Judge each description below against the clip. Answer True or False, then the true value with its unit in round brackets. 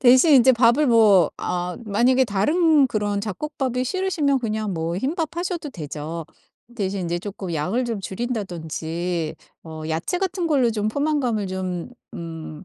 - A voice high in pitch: True (215 Hz)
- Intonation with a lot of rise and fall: True (7.0 semitones)